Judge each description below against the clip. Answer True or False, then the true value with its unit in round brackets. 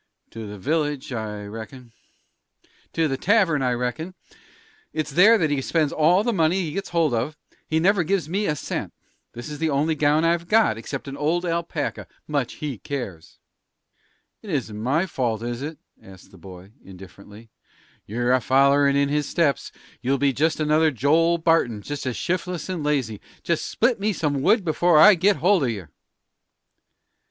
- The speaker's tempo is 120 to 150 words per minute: False (175 wpm)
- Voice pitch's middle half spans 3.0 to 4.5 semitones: False (5.3 semitones)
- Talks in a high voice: False (150 Hz)